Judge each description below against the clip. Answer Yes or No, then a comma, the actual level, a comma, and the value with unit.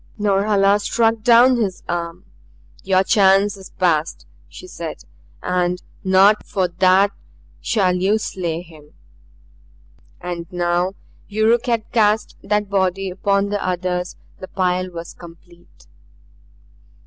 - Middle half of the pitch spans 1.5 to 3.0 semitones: Yes, narrow, 2.6 semitones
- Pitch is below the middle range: No, high, 190 Hz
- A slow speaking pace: Yes, slow, 115 wpm